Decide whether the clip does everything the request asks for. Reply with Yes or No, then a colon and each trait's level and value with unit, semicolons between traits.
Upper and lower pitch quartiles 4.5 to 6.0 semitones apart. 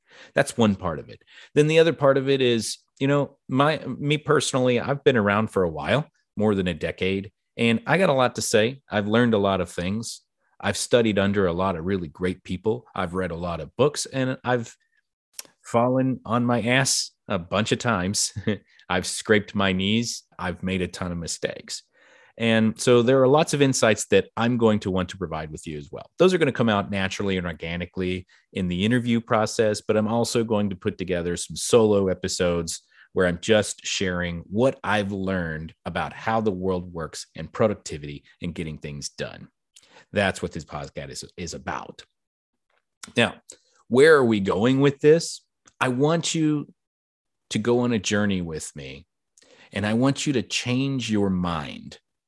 Yes: average, 5.2 semitones